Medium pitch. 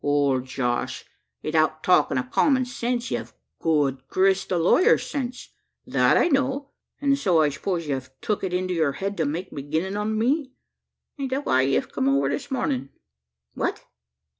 Yes: medium, 180 Hz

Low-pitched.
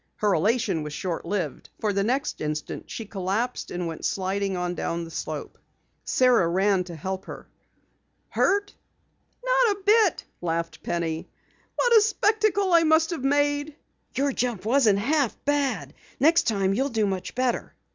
No: high, 225 Hz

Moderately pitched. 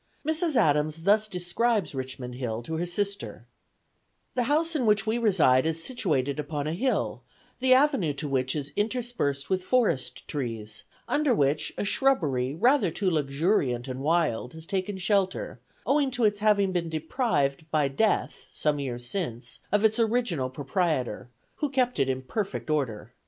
Yes: medium, 165 Hz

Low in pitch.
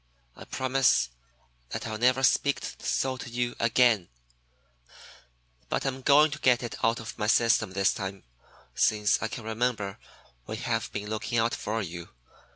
Yes: low, 115 Hz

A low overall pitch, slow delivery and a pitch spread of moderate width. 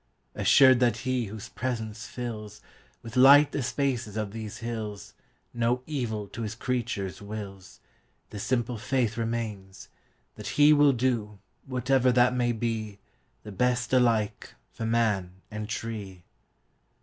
Yes: low, 115 Hz; slow, 115 wpm; average, 3.0 semitones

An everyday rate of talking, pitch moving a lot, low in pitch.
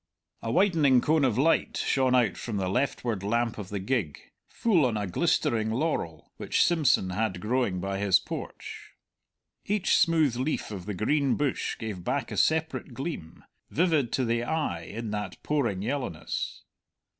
Yes: average, 160 wpm; wide, 6.1 semitones; low, 120 Hz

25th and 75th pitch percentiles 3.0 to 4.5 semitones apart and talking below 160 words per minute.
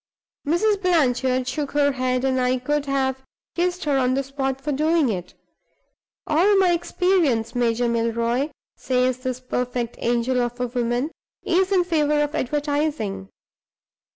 Yes: average, 3.6 semitones; average, 140 wpm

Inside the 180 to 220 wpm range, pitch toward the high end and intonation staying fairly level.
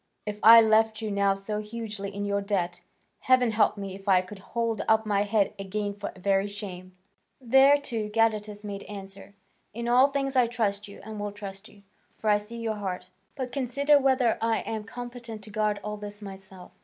Yes: average, 195 wpm; high, 210 Hz; narrow, 2.3 semitones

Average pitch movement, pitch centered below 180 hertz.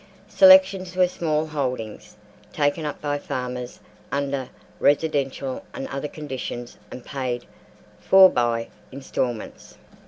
Yes: average, 3.7 semitones; medium, 140 Hz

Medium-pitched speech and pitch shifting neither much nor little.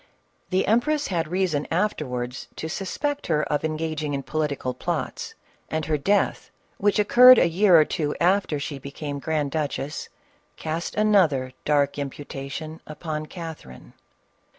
Yes: medium, 155 Hz; average, 4.2 semitones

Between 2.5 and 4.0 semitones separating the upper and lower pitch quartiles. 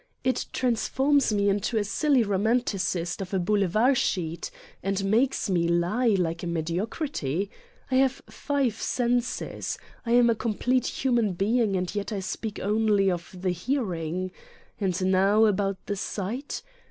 No: average, 4.6 semitones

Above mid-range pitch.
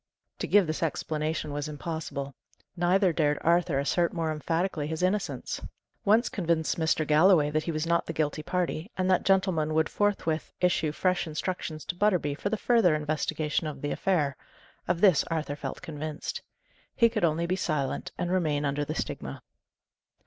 No: medium, 160 Hz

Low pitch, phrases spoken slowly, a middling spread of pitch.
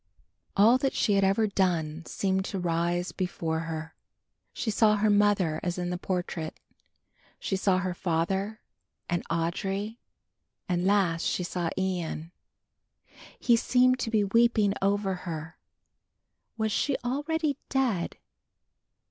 No: high, 190 Hz; slow, 130 wpm; average, 3.8 semitones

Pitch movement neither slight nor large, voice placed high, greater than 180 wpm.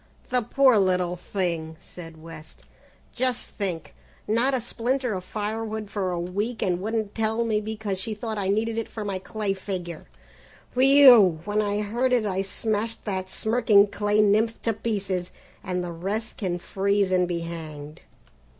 No: average, 3.4 semitones; high, 205 Hz; average, 165 wpm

